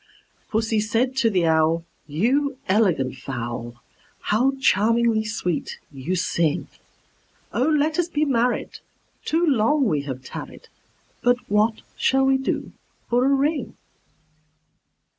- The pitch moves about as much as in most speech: No, wide, 8.3 semitones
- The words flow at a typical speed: No, slow, 120 wpm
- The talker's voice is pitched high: Yes, high, 225 Hz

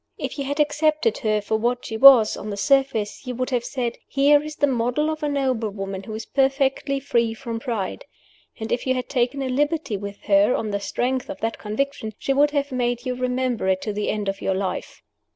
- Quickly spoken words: Yes, fast, 225 wpm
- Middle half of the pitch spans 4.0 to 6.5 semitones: Yes, average, 4.3 semitones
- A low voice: No, very high, 250 Hz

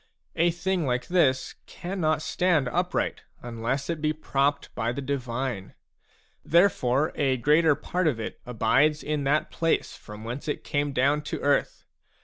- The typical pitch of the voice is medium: Yes, medium, 145 Hz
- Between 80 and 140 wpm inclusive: No, average, 150 wpm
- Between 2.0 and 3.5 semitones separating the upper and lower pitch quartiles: No, average, 3.9 semitones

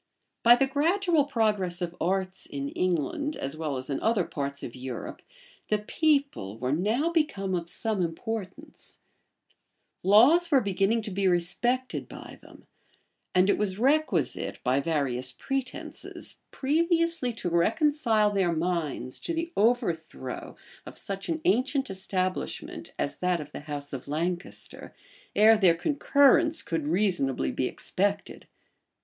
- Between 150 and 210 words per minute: No, slow, 135 wpm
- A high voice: Yes, high, 195 Hz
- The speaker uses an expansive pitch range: Yes, wide, 8.2 semitones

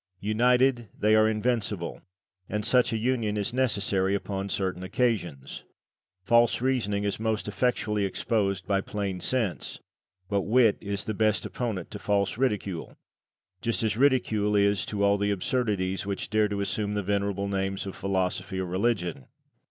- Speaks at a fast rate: No, average, 150 wpm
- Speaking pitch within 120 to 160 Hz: No, low, 105 Hz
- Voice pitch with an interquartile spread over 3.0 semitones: No, narrow, 2.5 semitones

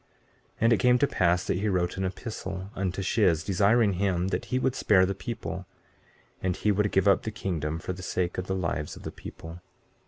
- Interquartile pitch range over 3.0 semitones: No, narrow, 2.6 semitones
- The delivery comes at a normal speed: No, fast, 220 wpm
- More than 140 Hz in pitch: No, very low, 95 Hz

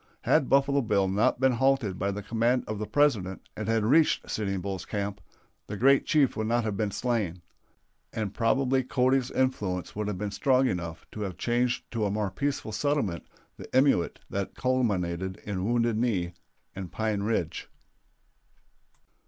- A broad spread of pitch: No, average, 4.5 semitones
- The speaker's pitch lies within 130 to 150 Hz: No, low, 110 Hz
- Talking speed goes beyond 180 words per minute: No, average, 165 wpm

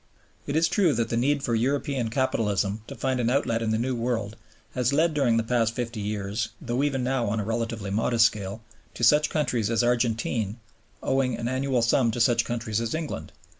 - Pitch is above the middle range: No, low, 120 Hz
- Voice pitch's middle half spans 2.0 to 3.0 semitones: Yes, average, 2.7 semitones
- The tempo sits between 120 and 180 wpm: No, fast, 205 wpm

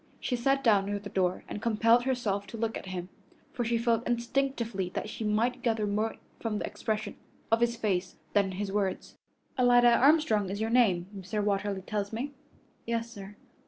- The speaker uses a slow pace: No, average, 190 wpm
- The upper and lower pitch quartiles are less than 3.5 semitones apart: Yes, average, 2.9 semitones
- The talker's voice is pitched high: Yes, high, 220 Hz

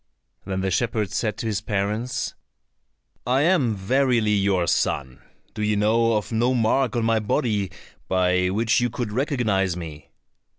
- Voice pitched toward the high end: No, low, 110 Hz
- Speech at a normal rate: Yes, average, 155 wpm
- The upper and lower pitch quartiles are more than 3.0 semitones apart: Yes, average, 3.8 semitones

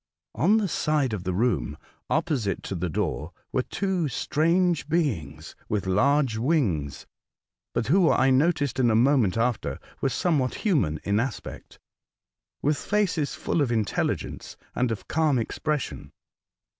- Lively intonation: Yes, wide, 6.7 semitones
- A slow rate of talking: No, average, 145 wpm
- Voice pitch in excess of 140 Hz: No, low, 130 Hz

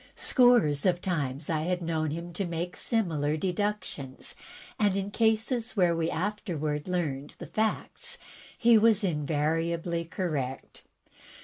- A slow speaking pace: Yes, slow, 125 wpm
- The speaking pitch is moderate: Yes, medium, 170 Hz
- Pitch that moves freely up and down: No, average, 5.0 semitones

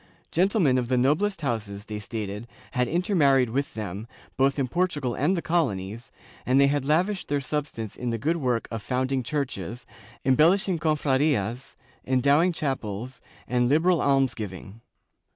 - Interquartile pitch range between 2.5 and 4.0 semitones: No, average, 4.8 semitones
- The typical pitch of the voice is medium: No, low, 130 Hz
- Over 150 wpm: No, average, 145 wpm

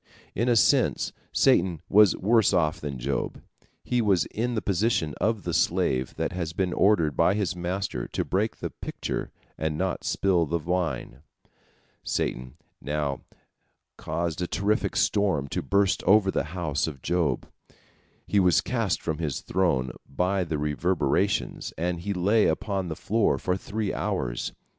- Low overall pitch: Yes, very low, 90 Hz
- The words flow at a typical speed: Yes, average, 155 wpm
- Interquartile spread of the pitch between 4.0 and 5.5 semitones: Yes, average, 4.3 semitones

